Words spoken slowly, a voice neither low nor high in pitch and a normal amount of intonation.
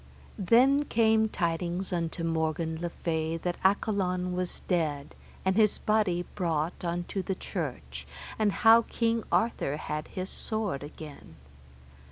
Yes: slow, 130 wpm; medium, 180 Hz; average, 4.5 semitones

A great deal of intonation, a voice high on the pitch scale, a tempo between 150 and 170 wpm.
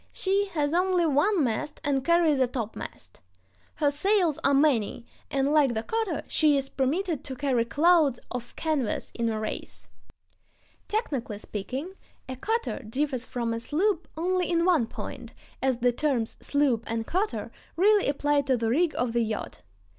Yes: wide, 5.8 semitones; very high, 285 Hz; average, 160 wpm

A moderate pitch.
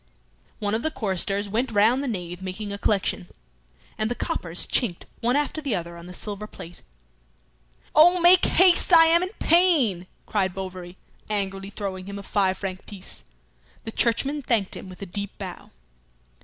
No: high, 205 Hz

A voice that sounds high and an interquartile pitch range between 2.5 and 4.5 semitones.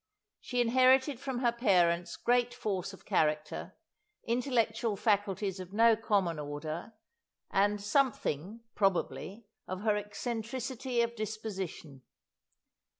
Yes: high, 215 Hz; average, 4.1 semitones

